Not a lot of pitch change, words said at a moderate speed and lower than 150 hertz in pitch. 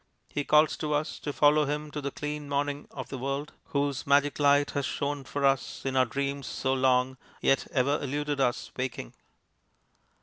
Yes: narrow, 1.5 semitones; average, 180 wpm; medium, 140 Hz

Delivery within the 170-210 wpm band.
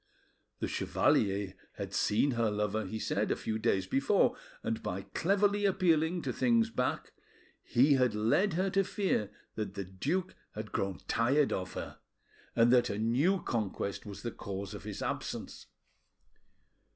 No: average, 155 wpm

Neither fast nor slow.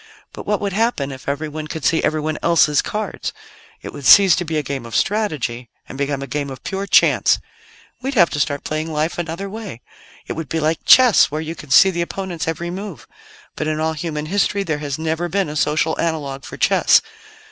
No: fast, 210 wpm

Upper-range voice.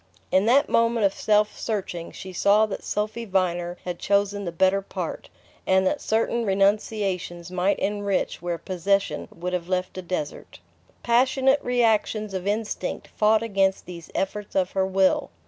Yes: high, 195 Hz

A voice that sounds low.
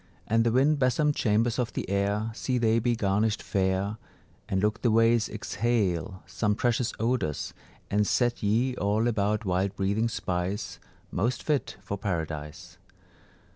Yes: low, 110 Hz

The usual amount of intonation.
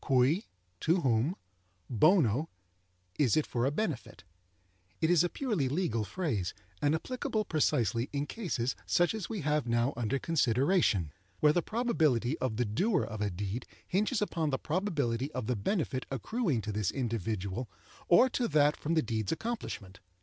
No: wide, 7.1 semitones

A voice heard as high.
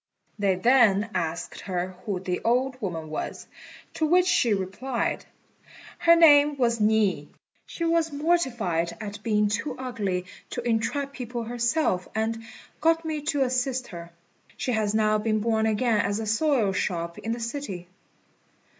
Yes: high, 225 Hz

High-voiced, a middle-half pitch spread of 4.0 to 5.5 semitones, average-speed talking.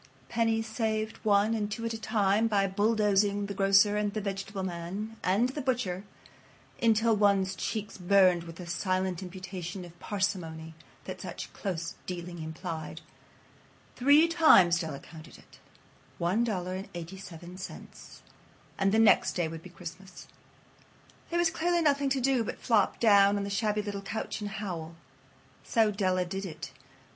No: high, 200 Hz; average, 3.4 semitones; average, 160 wpm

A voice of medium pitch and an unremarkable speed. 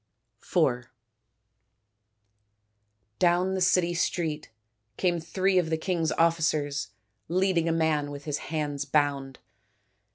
No: medium, 160 Hz; slow, 105 wpm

